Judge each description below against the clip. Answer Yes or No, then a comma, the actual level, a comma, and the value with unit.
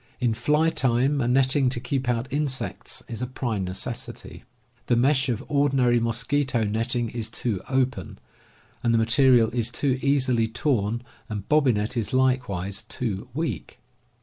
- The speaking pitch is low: Yes, low, 125 Hz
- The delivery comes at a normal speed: Yes, average, 155 wpm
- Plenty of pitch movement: No, average, 2.7 semitones